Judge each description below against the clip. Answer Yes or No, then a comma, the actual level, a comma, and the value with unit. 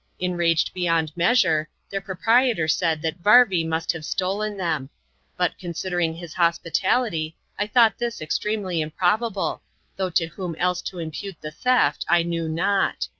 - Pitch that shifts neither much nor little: Yes, average, 3.4 semitones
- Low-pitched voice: No, medium, 175 Hz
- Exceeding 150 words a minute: No, average, 145 wpm